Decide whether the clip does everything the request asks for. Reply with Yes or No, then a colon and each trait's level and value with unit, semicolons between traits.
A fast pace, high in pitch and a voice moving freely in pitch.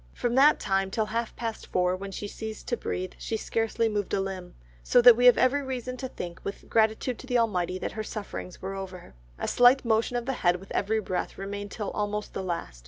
No: fast, 230 wpm; high, 215 Hz; average, 3.7 semitones